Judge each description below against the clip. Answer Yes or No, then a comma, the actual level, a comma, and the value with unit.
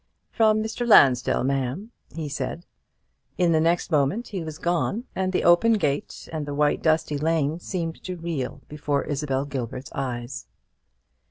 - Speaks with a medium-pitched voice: Yes, medium, 155 Hz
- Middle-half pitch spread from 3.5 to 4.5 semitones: Yes, average, 4.2 semitones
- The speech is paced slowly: No, average, 155 wpm